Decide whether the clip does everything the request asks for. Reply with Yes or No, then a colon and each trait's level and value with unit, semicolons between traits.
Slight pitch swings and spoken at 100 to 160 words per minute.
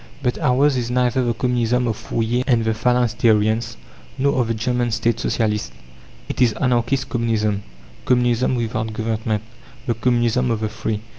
Yes: narrow, 1.9 semitones; average, 155 wpm